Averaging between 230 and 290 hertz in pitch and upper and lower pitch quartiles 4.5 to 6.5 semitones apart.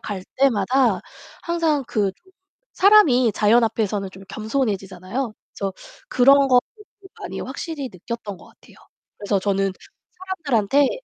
Yes: high, 235 Hz; wide, 5.6 semitones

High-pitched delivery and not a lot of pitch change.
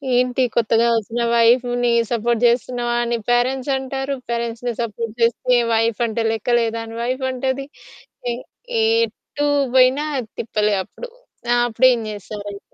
Yes: high, 240 Hz; narrow, 1.9 semitones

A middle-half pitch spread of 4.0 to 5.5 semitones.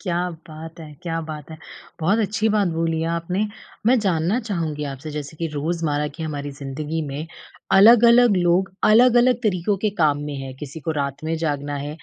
Yes: average, 4.7 semitones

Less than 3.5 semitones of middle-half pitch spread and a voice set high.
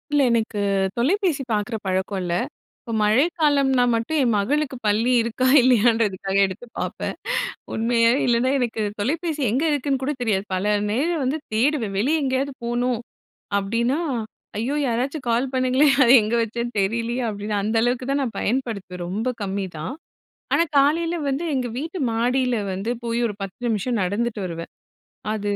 No: average, 4.2 semitones; high, 235 Hz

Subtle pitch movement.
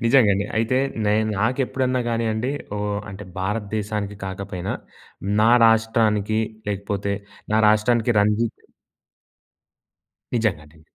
Yes: narrow, 2.0 semitones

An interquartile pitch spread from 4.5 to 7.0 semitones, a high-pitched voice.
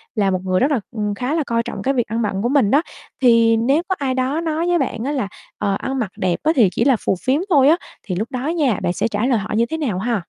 Yes: average, 4.8 semitones; high, 245 Hz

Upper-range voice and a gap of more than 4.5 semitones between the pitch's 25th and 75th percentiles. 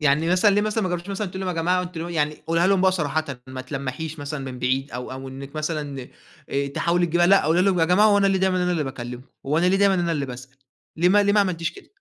No: medium, 165 Hz; average, 4.9 semitones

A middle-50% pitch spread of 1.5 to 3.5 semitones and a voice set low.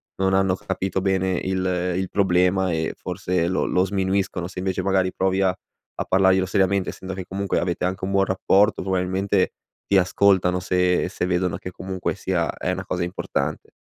No: narrow, 0.9 semitones; very low, 95 Hz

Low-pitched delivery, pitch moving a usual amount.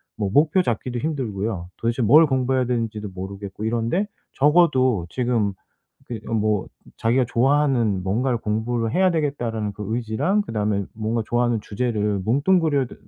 Yes: low, 115 Hz; average, 4.0 semitones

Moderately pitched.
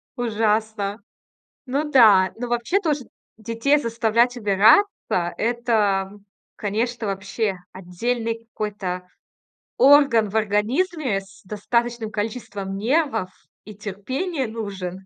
No: high, 220 Hz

